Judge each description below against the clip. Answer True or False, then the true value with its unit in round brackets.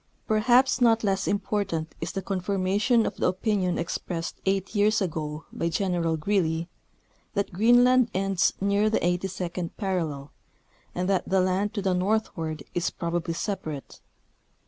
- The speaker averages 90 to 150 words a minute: True (140 wpm)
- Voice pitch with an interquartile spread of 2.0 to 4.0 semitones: True (3.4 semitones)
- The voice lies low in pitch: False (190 Hz)